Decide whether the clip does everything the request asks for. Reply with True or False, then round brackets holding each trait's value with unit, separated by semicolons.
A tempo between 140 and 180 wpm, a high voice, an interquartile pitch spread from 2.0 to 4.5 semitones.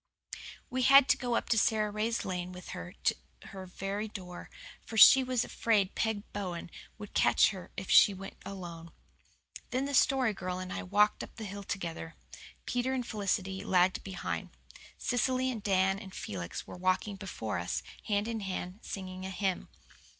True (170 wpm; 195 Hz; 3.3 semitones)